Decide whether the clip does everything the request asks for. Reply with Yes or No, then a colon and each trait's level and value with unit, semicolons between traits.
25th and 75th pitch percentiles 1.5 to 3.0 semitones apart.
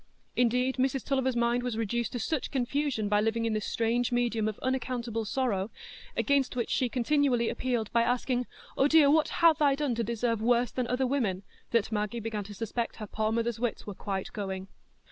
Yes: average, 2.7 semitones